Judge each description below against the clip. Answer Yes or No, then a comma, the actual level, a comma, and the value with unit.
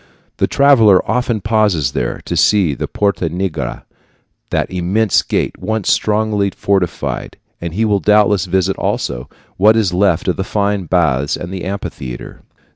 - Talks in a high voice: No, very low, 95 Hz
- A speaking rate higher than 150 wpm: No, average, 145 wpm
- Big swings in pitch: No, average, 3.4 semitones